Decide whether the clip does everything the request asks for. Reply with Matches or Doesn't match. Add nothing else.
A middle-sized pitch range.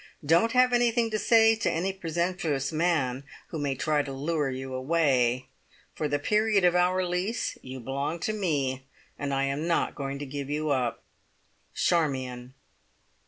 Matches